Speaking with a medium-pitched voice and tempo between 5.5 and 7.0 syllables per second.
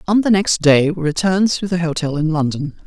Yes: medium, 170 Hz; 5.6 syllables/s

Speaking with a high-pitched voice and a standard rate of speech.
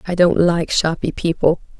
No: medium, 165 Hz; average, 165 wpm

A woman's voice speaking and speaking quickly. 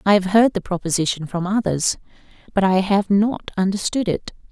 No: female; average, 175 wpm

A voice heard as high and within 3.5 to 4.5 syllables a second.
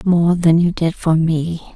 No: medium, 165 Hz; 3.6 syllables/s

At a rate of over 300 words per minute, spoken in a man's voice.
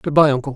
Yes: fast, 325 wpm; male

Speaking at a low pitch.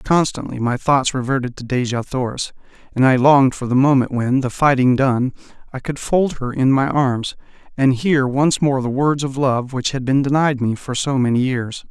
Yes: low, 130 Hz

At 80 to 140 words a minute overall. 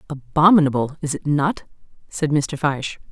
Yes: slow, 135 wpm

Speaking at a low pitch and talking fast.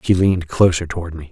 Yes: very low, 85 Hz; fast, 225 wpm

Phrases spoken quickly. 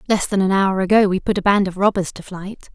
Yes: fast, 285 wpm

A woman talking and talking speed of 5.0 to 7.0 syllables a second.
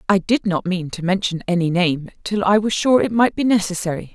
Yes: female; 5.5 syllables/s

